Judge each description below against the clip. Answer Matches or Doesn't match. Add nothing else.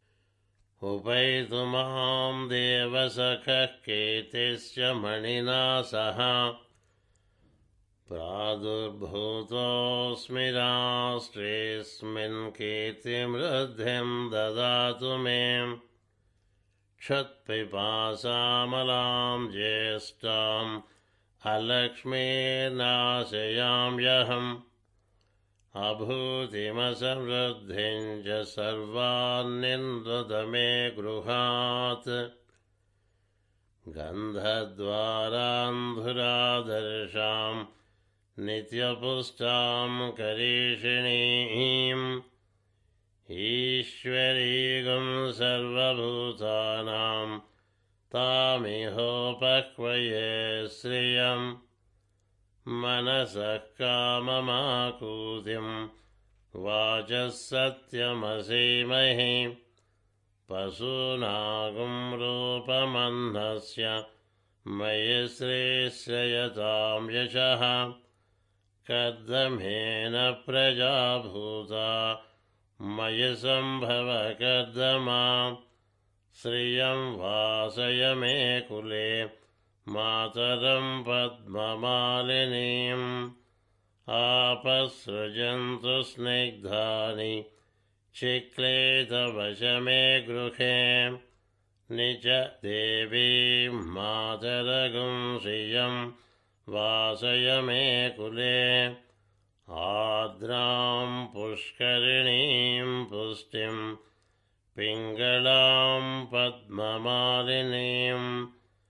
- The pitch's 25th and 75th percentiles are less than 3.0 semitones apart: Matches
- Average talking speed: Doesn't match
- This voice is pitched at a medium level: Doesn't match